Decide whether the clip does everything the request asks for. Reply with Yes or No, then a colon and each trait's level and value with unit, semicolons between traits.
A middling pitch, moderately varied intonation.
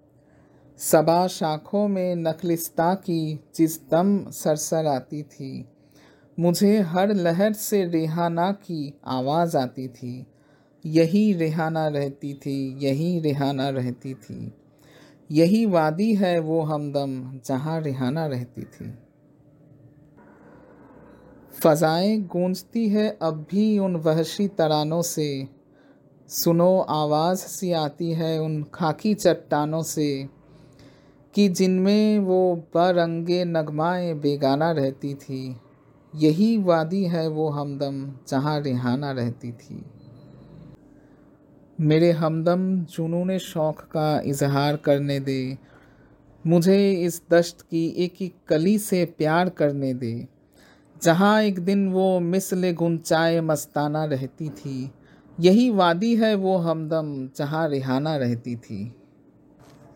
Yes: medium, 160 Hz; average, 3.7 semitones